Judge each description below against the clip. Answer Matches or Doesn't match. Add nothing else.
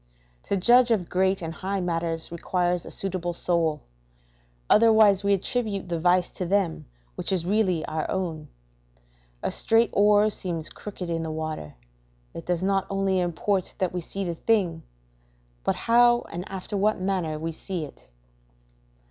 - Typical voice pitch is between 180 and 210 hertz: Matches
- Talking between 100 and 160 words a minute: Matches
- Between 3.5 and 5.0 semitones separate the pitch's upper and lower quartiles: Doesn't match